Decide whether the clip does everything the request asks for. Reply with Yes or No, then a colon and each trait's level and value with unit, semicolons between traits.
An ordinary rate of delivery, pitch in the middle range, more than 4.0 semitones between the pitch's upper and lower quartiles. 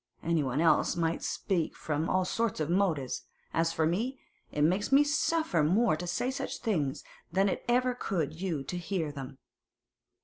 Yes: average, 170 wpm; medium, 170 Hz; average, 5.0 semitones